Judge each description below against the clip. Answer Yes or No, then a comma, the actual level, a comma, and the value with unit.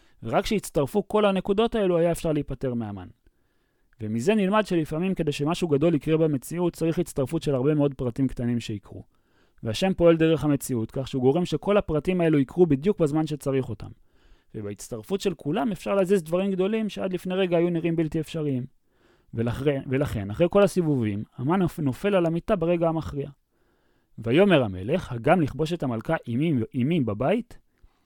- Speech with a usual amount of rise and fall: No, wide, 5.7 semitones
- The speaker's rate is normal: No, fast, 155 wpm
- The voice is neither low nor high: Yes, medium, 155 Hz